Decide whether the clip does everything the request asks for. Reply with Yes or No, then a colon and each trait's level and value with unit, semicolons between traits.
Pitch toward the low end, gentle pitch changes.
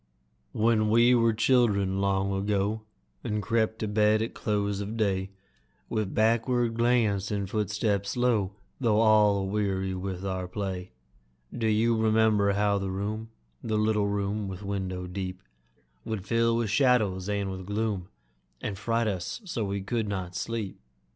Yes: low, 105 Hz; narrow, 2.3 semitones